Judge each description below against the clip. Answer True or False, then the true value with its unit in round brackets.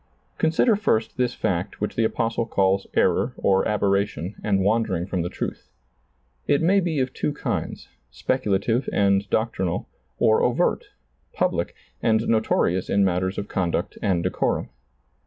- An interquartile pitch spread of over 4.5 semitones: False (3.5 semitones)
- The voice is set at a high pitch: False (100 Hz)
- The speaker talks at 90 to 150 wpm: True (140 wpm)